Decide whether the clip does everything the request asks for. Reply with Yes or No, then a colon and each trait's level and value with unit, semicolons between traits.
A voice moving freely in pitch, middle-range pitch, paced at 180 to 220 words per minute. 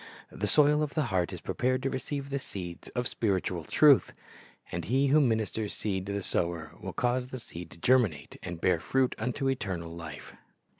No: wide, 6.9 semitones; low, 110 Hz; average, 190 wpm